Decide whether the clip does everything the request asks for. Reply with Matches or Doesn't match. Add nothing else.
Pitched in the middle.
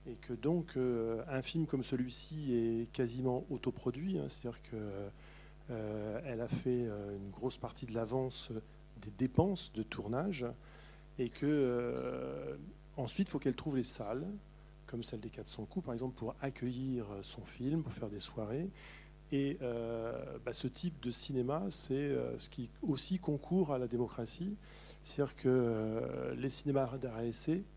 Doesn't match